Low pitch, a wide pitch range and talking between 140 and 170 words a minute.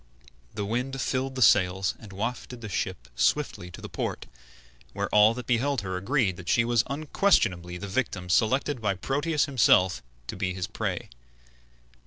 Yes: low, 110 Hz; wide, 5.8 semitones; average, 165 wpm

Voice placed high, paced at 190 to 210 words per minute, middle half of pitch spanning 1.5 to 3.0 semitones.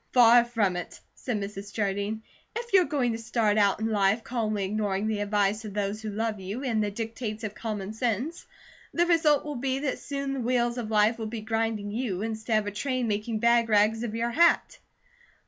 Yes: high, 220 Hz; fast, 205 wpm; narrow, 2.6 semitones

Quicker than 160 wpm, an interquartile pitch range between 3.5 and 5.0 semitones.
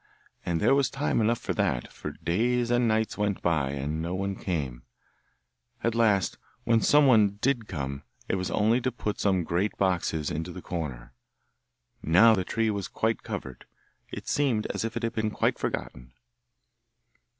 No: average, 170 wpm; wide, 5.5 semitones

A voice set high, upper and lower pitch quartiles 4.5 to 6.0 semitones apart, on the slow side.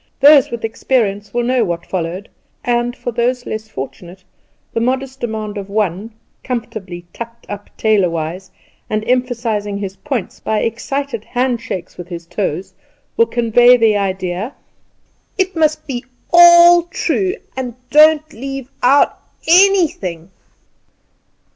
Yes: high, 230 Hz; average, 4.9 semitones; slow, 130 wpm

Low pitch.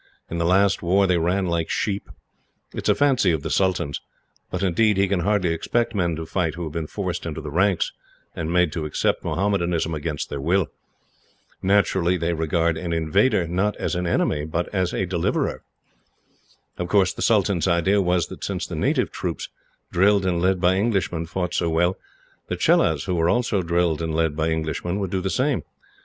Yes: very low, 90 Hz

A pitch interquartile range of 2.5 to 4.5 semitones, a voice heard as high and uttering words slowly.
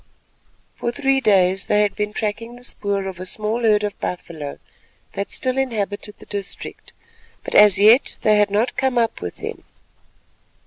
No: average, 2.8 semitones; high, 210 Hz; average, 170 wpm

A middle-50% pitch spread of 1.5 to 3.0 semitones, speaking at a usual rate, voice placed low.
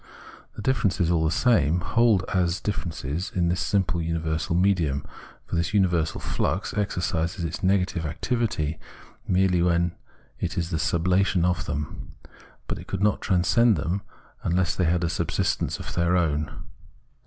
Yes: average, 2.7 semitones; average, 150 wpm; very low, 85 Hz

